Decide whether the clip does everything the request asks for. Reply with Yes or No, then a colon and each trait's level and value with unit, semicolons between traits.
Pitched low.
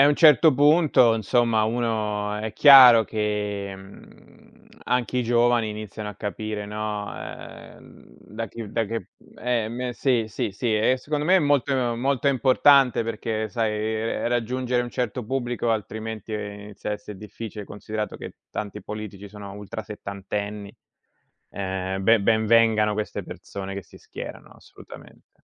Yes: low, 110 Hz